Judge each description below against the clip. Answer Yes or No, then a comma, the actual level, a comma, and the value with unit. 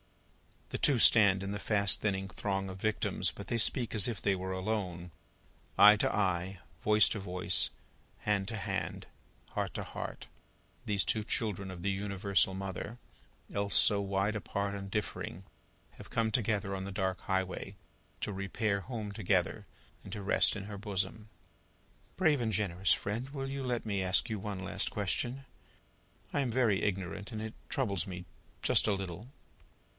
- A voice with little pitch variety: Yes, narrow, 2.2 semitones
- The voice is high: No, low, 100 Hz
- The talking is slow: No, average, 170 wpm